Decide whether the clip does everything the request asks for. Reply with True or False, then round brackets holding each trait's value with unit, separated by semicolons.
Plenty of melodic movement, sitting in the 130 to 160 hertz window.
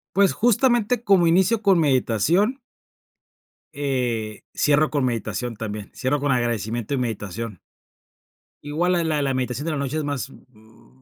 True (6.5 semitones; 140 Hz)